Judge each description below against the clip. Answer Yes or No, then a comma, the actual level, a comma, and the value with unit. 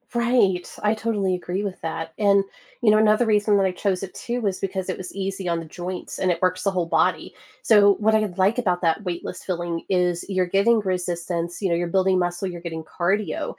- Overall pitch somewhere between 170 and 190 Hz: Yes, medium, 185 Hz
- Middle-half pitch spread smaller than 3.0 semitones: Yes, narrow, 2.6 semitones